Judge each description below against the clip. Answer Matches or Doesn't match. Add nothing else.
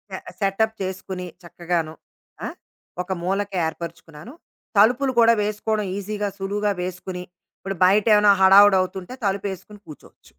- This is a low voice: Doesn't match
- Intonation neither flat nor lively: Doesn't match